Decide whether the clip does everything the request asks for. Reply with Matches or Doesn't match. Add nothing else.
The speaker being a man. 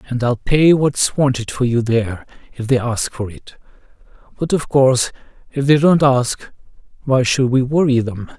Matches